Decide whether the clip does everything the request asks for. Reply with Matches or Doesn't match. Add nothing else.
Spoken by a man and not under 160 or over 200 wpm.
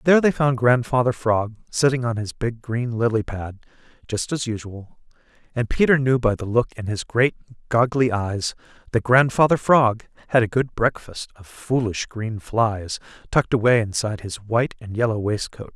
Matches